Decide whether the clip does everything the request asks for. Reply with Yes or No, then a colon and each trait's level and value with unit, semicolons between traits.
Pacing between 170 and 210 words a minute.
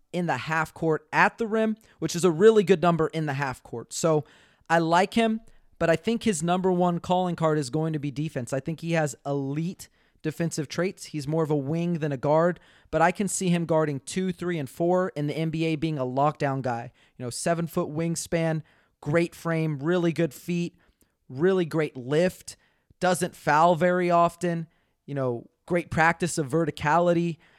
Yes: average, 195 wpm